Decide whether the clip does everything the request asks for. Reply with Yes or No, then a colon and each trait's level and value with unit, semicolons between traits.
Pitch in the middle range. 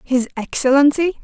No: very high, 270 Hz